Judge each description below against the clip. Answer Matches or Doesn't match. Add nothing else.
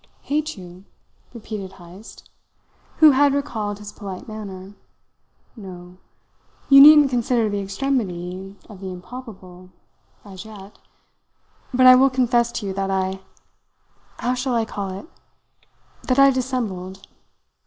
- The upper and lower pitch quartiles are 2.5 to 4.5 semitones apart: Doesn't match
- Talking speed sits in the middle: Doesn't match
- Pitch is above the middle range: Matches